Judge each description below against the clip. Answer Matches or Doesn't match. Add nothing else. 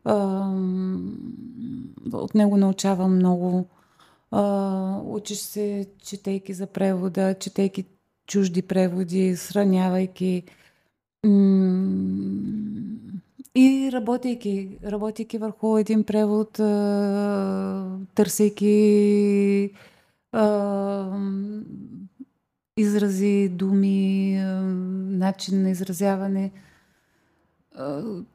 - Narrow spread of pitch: Matches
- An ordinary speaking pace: Doesn't match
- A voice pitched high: Matches